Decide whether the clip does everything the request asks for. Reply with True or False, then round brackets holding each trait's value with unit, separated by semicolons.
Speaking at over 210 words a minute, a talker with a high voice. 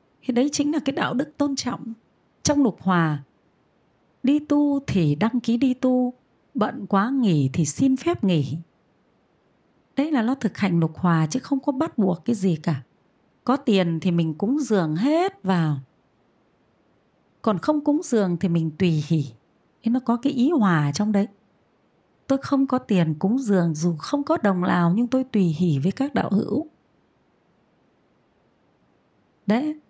False (170 wpm; 215 Hz)